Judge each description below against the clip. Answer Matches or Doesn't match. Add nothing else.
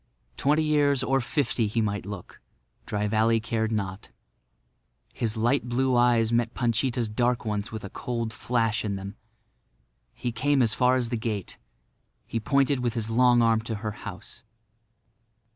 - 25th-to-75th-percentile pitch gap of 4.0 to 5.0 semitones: Doesn't match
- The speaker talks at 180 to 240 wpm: Doesn't match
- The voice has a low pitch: Matches